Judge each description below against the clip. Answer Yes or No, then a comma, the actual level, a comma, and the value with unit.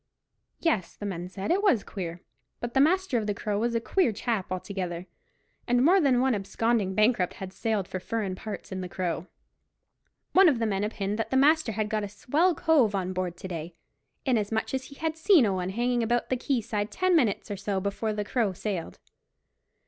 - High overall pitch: Yes, high, 215 Hz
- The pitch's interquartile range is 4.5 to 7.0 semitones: Yes, average, 4.9 semitones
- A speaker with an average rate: No, fast, 210 wpm